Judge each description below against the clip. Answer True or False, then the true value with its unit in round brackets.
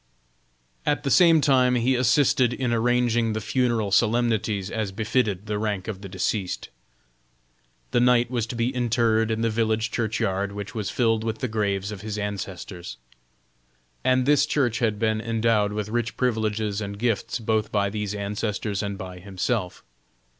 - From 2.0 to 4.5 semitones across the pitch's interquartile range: True (2.6 semitones)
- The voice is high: False (110 Hz)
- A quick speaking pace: False (160 wpm)